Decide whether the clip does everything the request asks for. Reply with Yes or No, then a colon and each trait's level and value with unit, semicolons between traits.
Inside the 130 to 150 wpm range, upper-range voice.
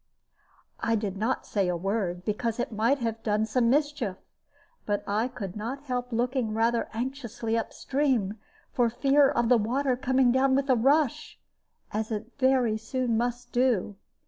No: average, 165 wpm; high, 235 Hz